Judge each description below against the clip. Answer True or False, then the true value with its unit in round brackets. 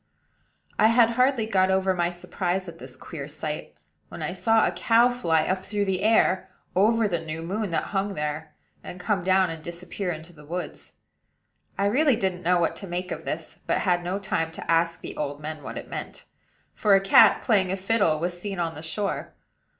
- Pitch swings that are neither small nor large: True (3.6 semitones)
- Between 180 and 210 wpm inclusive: True (205 wpm)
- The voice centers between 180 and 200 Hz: True (185 Hz)